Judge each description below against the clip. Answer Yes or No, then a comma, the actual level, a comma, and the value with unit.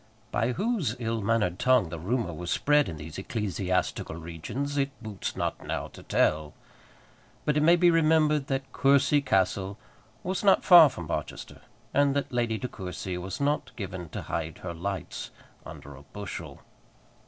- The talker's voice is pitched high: No, low, 110 Hz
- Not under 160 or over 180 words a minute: Yes, average, 165 wpm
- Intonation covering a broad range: Yes, wide, 8.1 semitones